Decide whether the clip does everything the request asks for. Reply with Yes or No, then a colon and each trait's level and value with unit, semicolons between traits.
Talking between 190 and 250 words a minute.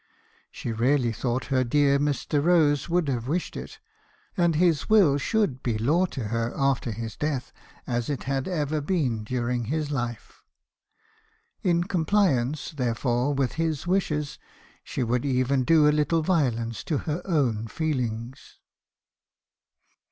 No: average, 140 wpm